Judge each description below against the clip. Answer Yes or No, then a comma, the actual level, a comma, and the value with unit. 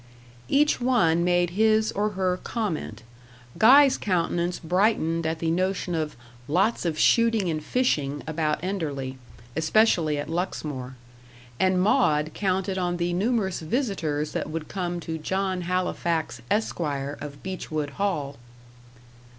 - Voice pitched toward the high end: No, medium, 175 Hz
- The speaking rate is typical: No, slow, 125 wpm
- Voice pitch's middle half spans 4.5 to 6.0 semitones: No, average, 4.1 semitones